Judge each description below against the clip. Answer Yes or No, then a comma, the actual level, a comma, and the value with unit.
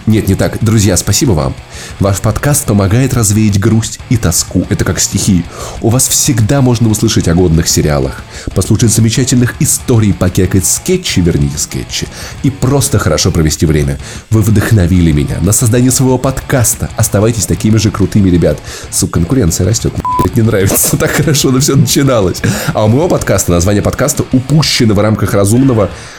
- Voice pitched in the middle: No, low, 110 Hz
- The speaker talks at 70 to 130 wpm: No, fast, 160 wpm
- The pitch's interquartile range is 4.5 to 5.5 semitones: Yes, average, 4.9 semitones